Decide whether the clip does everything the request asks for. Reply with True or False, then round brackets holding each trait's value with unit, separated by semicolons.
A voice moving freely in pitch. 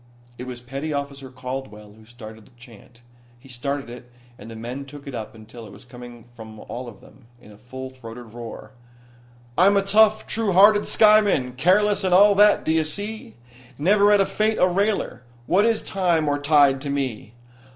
True (8.1 semitones)